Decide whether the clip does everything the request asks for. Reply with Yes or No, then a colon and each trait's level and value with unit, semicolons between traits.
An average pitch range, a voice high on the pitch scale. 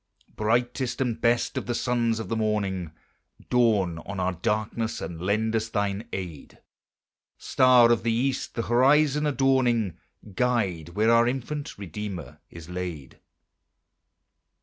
No: average, 4.2 semitones; low, 110 Hz